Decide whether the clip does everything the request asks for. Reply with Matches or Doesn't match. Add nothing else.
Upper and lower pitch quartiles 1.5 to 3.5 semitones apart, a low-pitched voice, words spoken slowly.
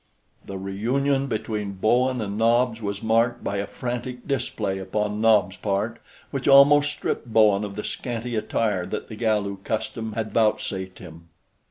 Doesn't match